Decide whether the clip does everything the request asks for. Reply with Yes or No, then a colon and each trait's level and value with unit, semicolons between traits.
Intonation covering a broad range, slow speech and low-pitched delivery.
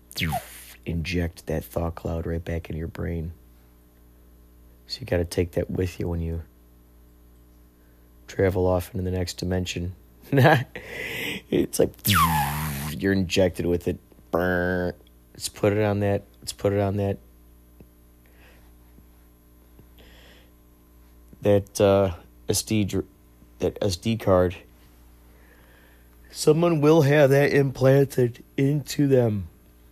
Yes: wide, 8.2 semitones; slow, 110 wpm; very low, 80 Hz